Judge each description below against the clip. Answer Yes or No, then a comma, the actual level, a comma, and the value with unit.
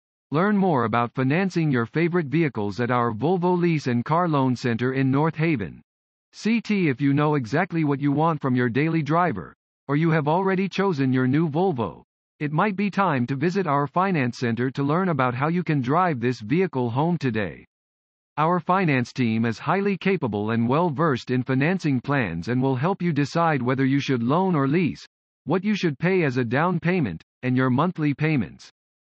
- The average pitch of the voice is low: No, medium, 145 Hz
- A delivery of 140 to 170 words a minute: No, average, 190 wpm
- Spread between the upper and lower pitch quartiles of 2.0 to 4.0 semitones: No, wide, 5.6 semitones